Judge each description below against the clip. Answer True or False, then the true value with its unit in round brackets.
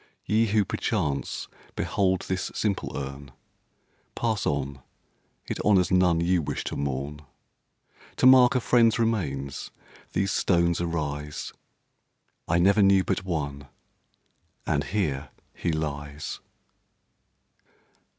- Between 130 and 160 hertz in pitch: False (85 Hz)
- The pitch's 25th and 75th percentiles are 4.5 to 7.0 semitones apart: True (5.5 semitones)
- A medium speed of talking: False (110 wpm)